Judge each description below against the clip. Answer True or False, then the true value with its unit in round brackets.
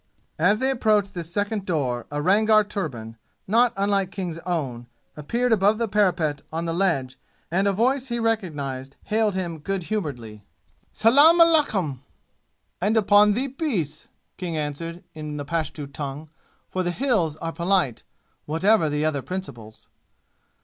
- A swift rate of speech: False (150 wpm)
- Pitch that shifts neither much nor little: False (6.1 semitones)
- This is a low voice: False (180 Hz)